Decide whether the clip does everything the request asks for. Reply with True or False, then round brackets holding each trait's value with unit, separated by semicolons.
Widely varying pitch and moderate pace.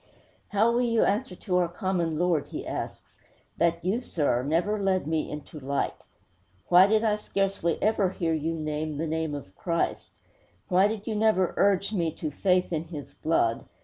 False (4.1 semitones; 180 wpm)